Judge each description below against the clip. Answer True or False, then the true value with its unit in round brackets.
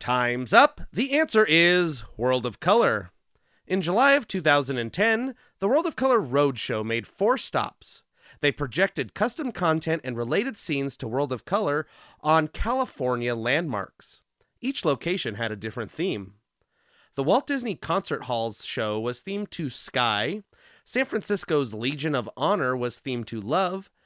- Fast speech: False (145 wpm)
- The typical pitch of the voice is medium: True (150 Hz)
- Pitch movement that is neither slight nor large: False (8.6 semitones)